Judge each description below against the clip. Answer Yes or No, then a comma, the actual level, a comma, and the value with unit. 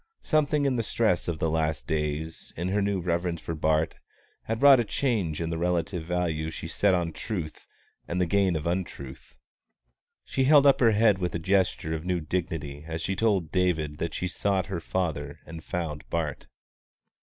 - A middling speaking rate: Yes, average, 190 wpm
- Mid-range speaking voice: No, very low, 85 Hz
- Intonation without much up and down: No, average, 3.7 semitones